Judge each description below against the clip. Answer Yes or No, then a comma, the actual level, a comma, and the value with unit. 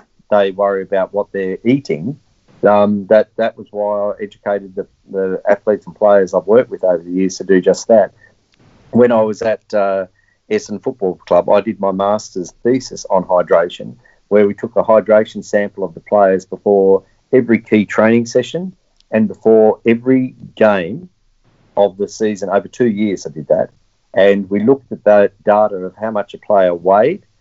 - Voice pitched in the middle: No, low, 105 Hz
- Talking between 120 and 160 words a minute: No, average, 180 wpm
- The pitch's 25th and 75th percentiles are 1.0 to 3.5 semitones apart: Yes, average, 2.7 semitones